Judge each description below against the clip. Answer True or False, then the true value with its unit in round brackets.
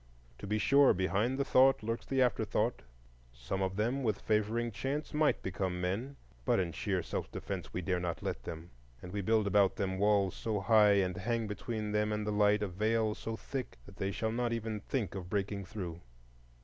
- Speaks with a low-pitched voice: True (105 Hz)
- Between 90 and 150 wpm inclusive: False (200 wpm)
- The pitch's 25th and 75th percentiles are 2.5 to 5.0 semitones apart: True (3.1 semitones)